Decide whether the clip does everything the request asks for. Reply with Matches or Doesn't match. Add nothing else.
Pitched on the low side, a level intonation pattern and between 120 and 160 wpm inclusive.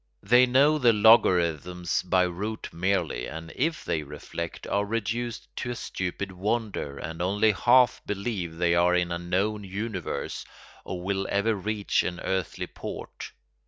Doesn't match